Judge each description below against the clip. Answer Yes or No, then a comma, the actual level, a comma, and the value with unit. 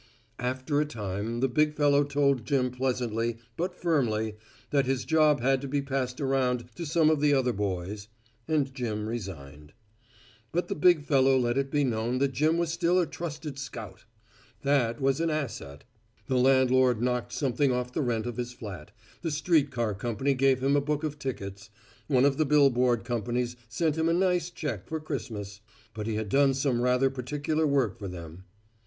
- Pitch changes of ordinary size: Yes, average, 3.8 semitones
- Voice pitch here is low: Yes, low, 130 Hz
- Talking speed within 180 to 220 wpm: Yes, average, 185 wpm